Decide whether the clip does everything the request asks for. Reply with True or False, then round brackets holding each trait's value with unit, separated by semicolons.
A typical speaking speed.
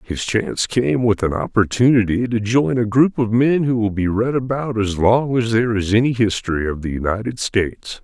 False (210 wpm)